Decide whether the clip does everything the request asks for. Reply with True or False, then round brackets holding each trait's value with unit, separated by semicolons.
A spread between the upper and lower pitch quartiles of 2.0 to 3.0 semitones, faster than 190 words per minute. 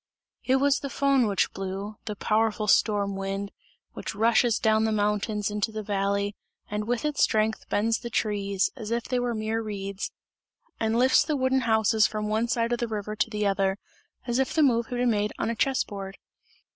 True (2.5 semitones; 200 wpm)